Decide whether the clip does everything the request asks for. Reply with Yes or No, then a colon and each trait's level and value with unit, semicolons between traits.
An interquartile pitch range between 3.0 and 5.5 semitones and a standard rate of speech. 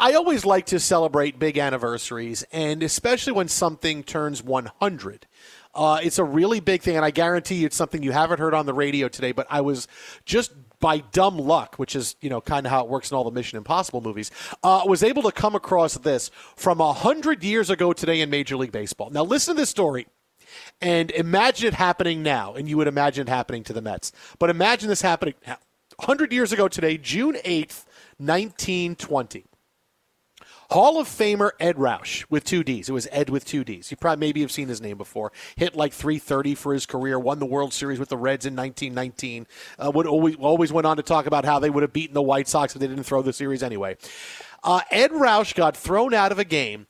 No: average, 5.2 semitones; fast, 220 wpm